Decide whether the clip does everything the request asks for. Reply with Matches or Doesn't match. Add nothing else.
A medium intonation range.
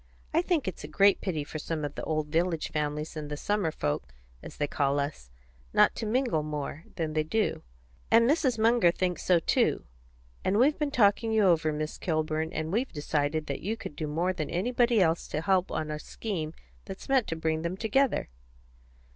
Doesn't match